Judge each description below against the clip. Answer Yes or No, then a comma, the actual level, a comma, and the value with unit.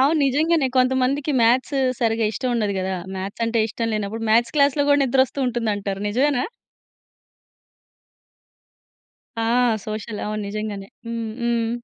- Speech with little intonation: No, average, 3.6 semitones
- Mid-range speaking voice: No, high, 235 Hz